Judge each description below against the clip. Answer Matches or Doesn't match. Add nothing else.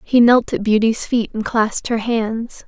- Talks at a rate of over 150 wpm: Matches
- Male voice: Doesn't match